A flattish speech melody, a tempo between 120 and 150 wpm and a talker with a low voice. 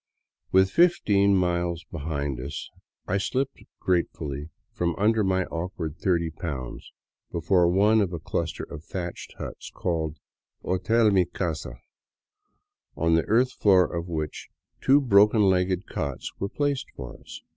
No: average, 3.5 semitones; average, 140 wpm; very low, 90 Hz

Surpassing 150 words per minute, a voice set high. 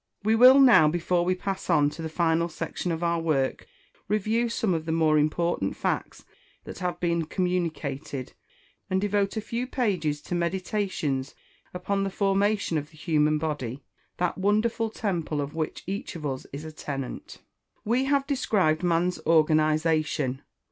No: average, 160 wpm; medium, 170 Hz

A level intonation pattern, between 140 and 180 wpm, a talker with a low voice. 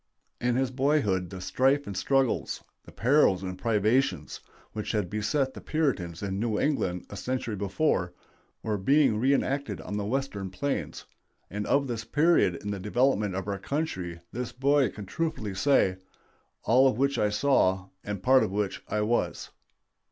No: wide, 5.6 semitones; average, 165 wpm; low, 110 Hz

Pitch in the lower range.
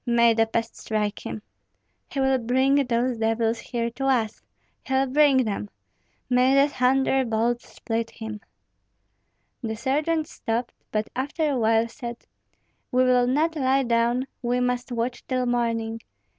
No: high, 245 Hz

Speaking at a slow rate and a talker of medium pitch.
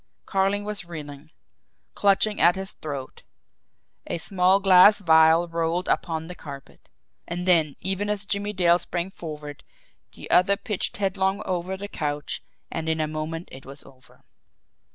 No: average, 155 wpm; medium, 175 Hz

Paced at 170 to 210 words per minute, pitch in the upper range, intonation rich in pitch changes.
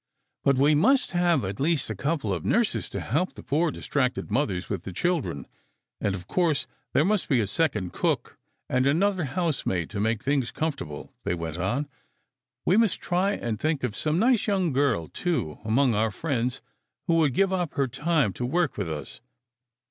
No: average, 190 wpm; medium, 140 Hz; wide, 7.9 semitones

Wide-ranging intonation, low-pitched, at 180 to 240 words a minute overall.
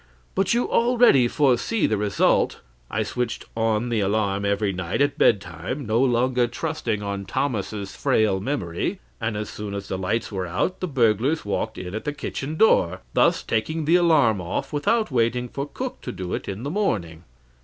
Yes: wide, 6.2 semitones; low, 115 Hz; average, 185 wpm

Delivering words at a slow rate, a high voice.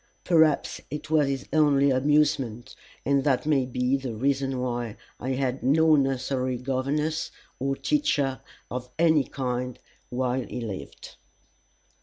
No: slow, 130 wpm; low, 135 Hz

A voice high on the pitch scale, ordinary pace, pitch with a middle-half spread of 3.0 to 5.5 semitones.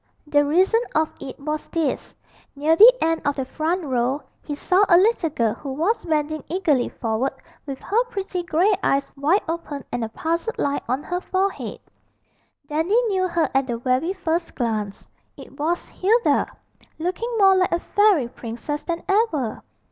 Yes: very high, 320 Hz; average, 170 wpm; average, 5.2 semitones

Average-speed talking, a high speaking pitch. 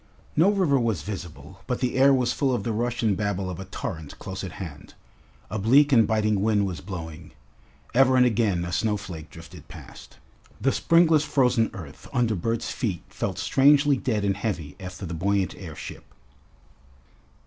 No: average, 170 wpm; low, 105 Hz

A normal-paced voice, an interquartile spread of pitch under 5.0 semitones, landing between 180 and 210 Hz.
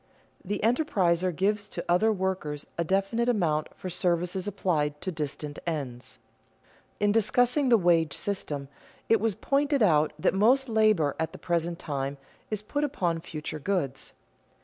No: average, 150 wpm; wide, 5.5 semitones; medium, 185 Hz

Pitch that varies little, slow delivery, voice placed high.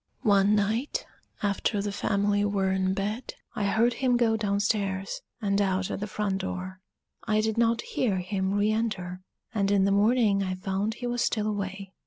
No: narrow, 2.0 semitones; average, 185 wpm; high, 205 Hz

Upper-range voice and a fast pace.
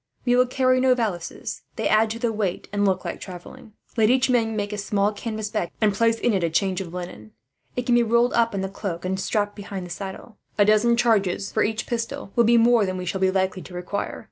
Yes: high, 210 Hz; fast, 245 wpm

